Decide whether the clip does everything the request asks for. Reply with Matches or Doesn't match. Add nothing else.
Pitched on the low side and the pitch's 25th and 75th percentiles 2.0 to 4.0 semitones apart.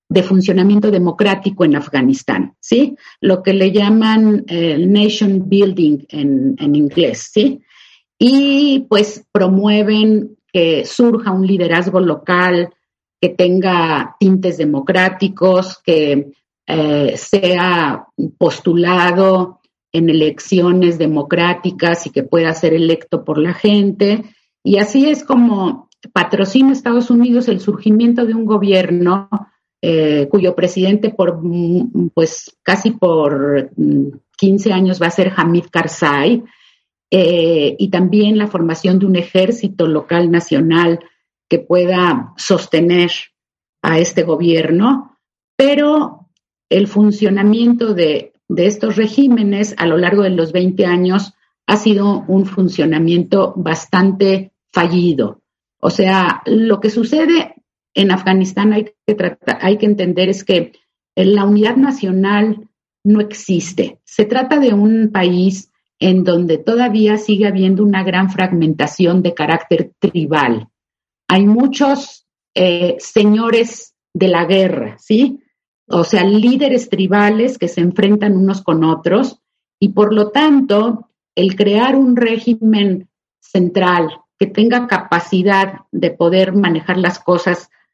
Doesn't match